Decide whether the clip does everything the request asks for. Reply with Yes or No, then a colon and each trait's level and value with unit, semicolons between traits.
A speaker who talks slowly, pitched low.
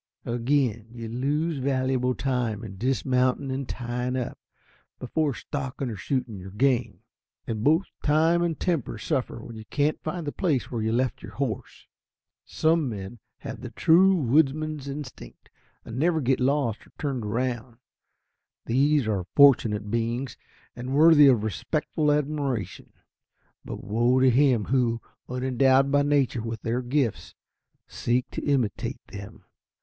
No: average, 145 wpm; low, 130 Hz